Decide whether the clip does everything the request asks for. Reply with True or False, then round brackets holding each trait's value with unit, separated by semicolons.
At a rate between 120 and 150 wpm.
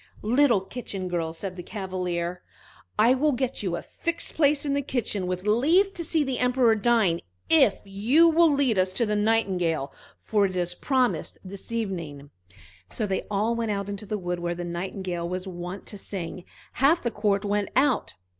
False (190 wpm)